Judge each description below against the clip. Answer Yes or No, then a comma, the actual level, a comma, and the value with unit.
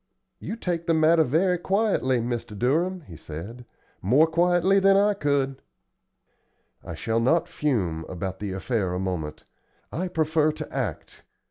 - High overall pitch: No, medium, 145 Hz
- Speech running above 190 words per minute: No, average, 145 wpm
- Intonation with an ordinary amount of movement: No, wide, 8.6 semitones